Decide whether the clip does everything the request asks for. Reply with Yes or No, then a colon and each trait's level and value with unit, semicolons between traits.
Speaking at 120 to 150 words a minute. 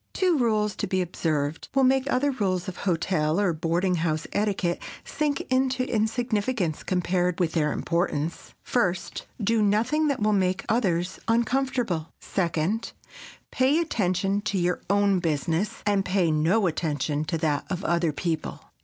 Yes: average, 145 wpm